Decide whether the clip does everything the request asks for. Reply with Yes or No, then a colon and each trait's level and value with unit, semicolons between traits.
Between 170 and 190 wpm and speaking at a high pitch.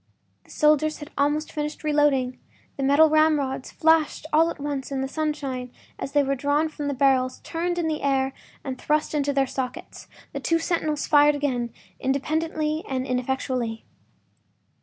No: average, 160 wpm; very high, 290 Hz